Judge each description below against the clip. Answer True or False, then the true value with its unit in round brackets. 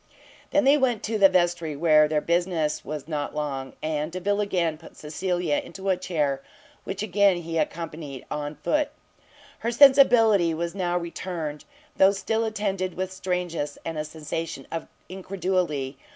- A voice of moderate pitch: True (175 Hz)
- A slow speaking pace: False (150 wpm)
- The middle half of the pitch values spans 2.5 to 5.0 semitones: True (4.1 semitones)